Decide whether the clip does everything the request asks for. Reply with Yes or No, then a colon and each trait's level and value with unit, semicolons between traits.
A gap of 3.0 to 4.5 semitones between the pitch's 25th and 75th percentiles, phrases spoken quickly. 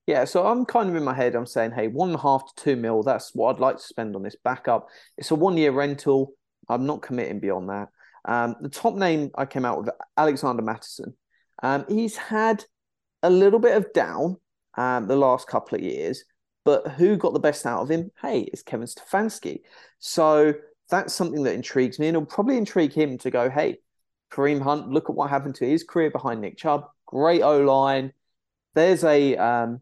No: average, 5.0 semitones; fast, 210 wpm